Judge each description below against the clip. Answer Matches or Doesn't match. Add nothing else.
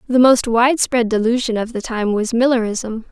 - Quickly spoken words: Doesn't match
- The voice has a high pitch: Matches